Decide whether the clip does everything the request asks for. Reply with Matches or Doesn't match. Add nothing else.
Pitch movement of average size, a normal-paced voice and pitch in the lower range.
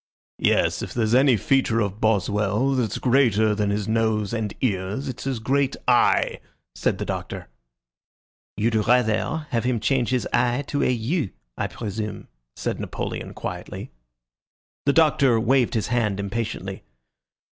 Matches